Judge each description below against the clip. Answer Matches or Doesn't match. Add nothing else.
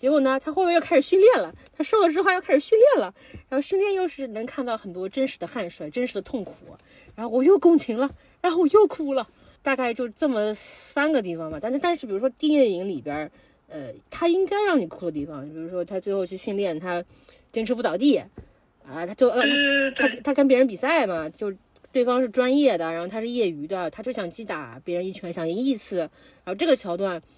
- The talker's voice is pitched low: Doesn't match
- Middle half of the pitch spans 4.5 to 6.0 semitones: Doesn't match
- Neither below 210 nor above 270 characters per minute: Doesn't match